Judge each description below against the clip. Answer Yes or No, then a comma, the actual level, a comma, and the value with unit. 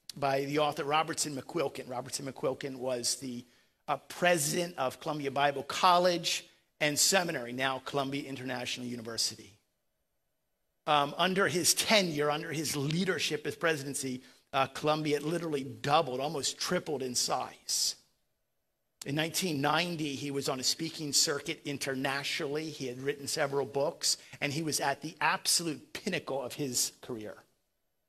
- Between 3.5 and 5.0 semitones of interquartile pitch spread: No, average, 2.9 semitones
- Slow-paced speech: Yes, slow, 130 wpm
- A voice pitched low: No, medium, 145 Hz